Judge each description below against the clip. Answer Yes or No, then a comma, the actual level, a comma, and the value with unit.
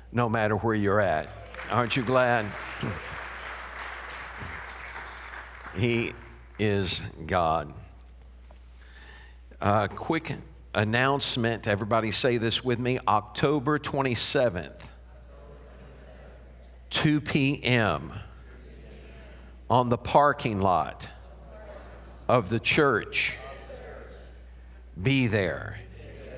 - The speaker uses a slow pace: Yes, slow, 75 wpm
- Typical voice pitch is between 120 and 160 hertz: No, low, 100 Hz